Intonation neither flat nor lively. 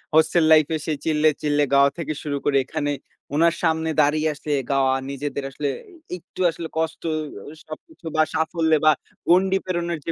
No: narrow, 2.2 semitones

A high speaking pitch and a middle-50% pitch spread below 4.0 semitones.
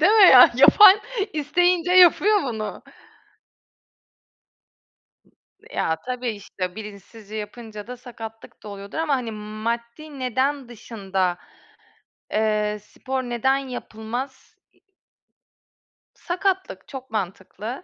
No: high, 240 Hz; average, 4.8 semitones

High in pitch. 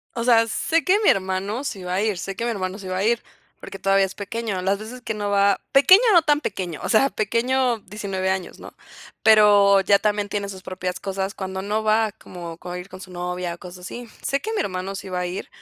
Yes: high, 200 Hz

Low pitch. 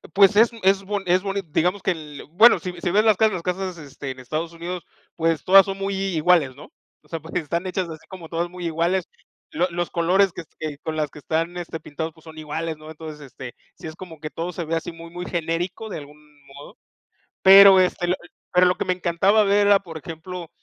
No: medium, 170 Hz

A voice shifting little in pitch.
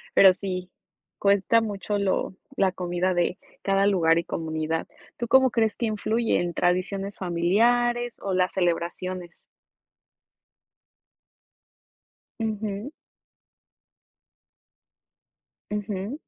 No: average, 3.2 semitones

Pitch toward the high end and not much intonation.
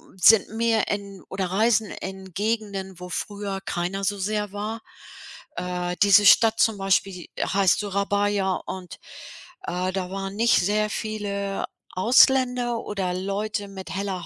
Yes: high, 200 Hz; narrow, 2.0 semitones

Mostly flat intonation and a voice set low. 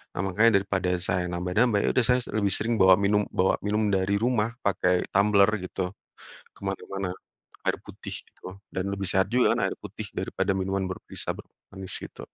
Yes: narrow, 2.0 semitones; low, 100 Hz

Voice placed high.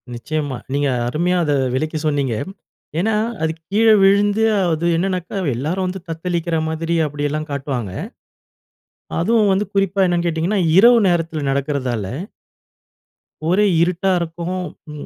No: medium, 165 Hz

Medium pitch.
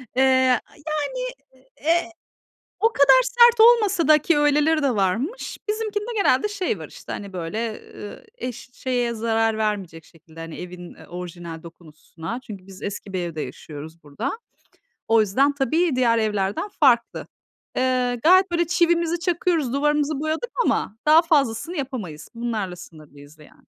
No: very high, 250 Hz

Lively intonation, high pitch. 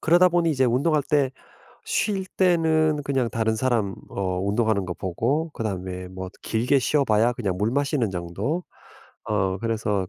No: wide, 7.2 semitones; low, 115 Hz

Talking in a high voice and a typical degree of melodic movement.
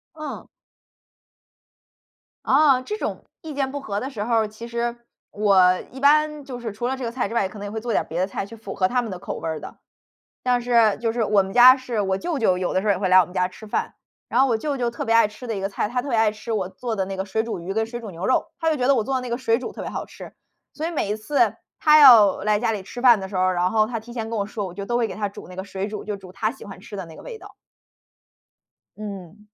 Yes: high, 220 Hz; average, 3.9 semitones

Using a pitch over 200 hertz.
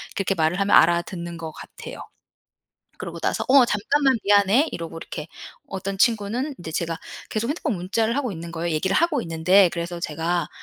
No: high, 190 Hz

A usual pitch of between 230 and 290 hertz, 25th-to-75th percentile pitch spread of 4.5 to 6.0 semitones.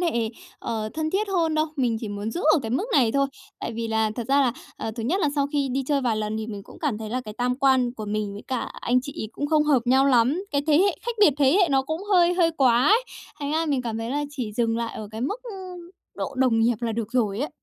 Yes: very high, 260 Hz; average, 5.2 semitones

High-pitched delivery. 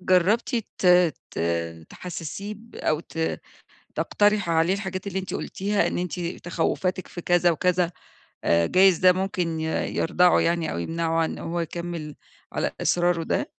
No: medium, 175 Hz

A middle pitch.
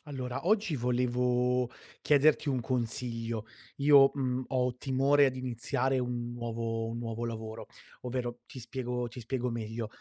No: low, 125 Hz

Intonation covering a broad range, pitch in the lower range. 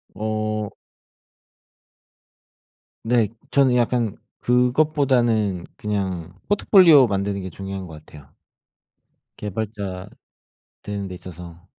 No: average, 4.6 semitones; low, 105 Hz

